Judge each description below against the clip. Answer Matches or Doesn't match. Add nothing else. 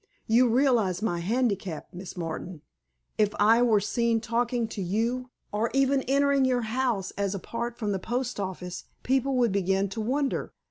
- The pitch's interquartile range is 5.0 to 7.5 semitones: Doesn't match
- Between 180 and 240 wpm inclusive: Doesn't match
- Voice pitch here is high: Matches